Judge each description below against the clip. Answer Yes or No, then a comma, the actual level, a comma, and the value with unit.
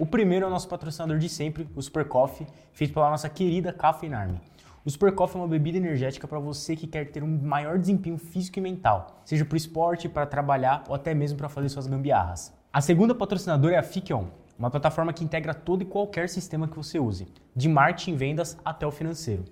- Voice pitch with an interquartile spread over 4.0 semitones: No, average, 3.2 semitones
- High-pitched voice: No, medium, 155 Hz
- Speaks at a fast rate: Yes, fast, 220 wpm